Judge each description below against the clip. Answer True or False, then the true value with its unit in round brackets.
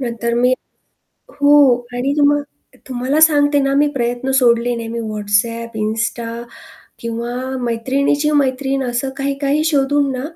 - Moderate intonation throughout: True (3.2 semitones)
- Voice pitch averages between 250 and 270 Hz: True (255 Hz)